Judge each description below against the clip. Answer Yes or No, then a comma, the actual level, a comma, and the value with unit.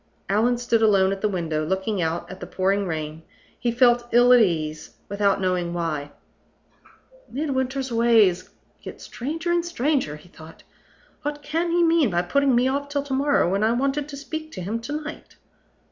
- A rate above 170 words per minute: Yes, average, 180 wpm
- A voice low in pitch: No, high, 230 Hz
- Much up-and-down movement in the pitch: Yes, wide, 7.3 semitones